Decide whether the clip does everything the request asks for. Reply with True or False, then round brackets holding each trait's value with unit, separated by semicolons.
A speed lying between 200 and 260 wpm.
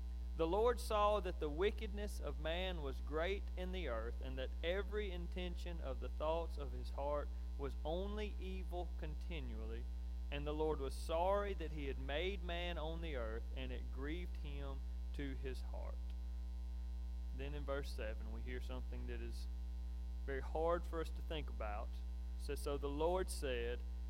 False (170 wpm)